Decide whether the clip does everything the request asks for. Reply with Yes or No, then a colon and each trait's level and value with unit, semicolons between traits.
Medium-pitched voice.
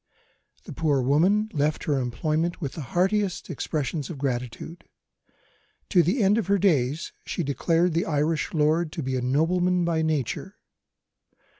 Yes: medium, 160 Hz